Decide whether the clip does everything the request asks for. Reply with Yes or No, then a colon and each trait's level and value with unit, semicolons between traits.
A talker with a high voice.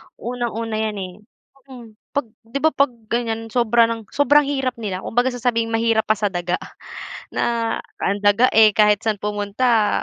Yes: high, 225 Hz